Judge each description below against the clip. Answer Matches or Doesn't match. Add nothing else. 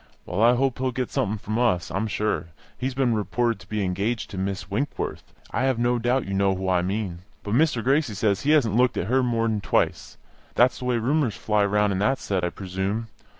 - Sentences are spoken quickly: Matches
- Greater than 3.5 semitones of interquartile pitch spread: Matches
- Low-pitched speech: Matches